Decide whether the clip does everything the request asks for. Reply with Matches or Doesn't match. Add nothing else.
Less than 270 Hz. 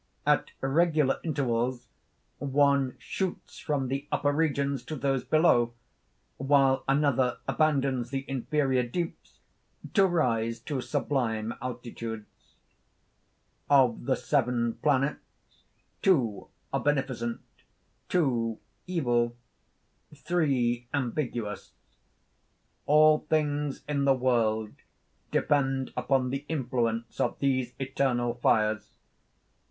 Matches